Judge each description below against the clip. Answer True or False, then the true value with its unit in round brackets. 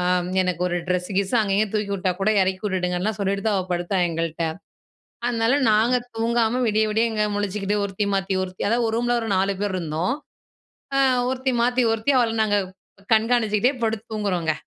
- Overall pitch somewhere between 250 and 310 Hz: False (205 Hz)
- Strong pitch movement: False (3.4 semitones)